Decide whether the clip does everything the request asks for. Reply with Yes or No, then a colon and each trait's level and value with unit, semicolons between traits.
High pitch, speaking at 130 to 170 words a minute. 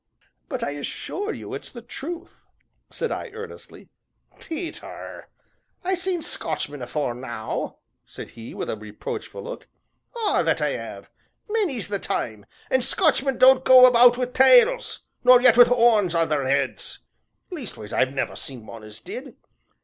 Yes: high, 245 Hz; average, 150 wpm